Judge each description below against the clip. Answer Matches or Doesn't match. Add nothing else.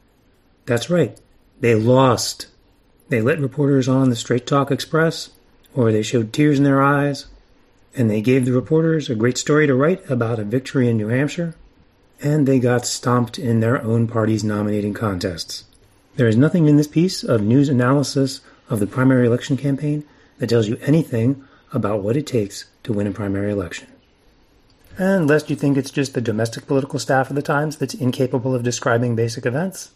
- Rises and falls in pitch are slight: Doesn't match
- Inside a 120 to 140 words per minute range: Doesn't match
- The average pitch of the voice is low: Matches